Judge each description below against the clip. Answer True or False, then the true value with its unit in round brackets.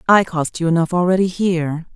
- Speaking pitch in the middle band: True (175 Hz)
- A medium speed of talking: True (185 wpm)